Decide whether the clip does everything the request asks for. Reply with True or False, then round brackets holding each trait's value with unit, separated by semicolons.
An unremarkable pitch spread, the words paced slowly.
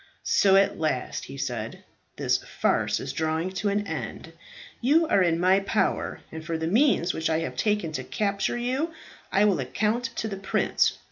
False (4.7 semitones; 185 wpm)